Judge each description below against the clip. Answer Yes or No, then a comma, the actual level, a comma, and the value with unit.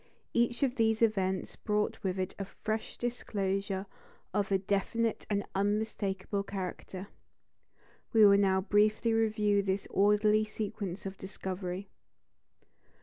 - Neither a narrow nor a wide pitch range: No, narrow, 2.0 semitones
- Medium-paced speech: No, slow, 120 wpm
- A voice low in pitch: No, high, 205 Hz